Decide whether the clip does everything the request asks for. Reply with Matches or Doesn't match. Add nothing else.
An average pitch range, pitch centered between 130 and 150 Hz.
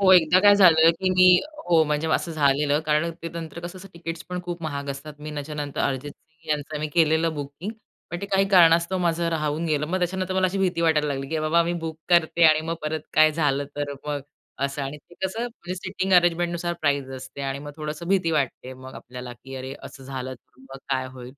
Doesn't match